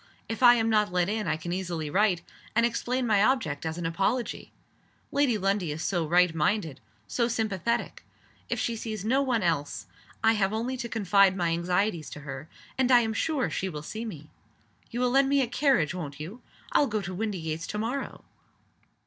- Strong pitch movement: Yes, wide, 5.7 semitones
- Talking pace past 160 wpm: Yes, average, 195 wpm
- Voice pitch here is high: Yes, high, 205 Hz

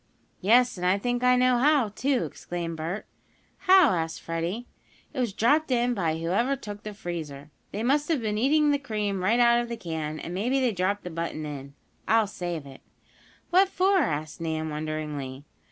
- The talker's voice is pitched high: Yes, high, 205 Hz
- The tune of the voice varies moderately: No, wide, 7.3 semitones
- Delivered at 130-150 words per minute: No, average, 185 wpm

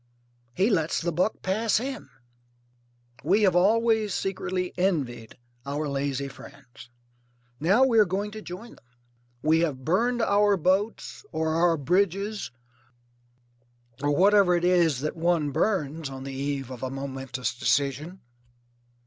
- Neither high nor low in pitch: Yes, medium, 170 Hz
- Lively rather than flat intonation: Yes, wide, 6.1 semitones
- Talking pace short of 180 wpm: Yes, slow, 135 wpm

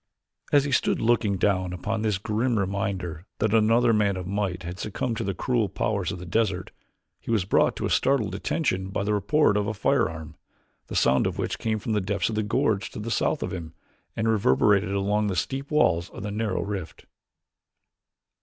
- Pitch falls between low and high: No, low, 105 Hz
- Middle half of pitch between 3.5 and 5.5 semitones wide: No, average, 2.9 semitones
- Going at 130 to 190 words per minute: No, average, 200 wpm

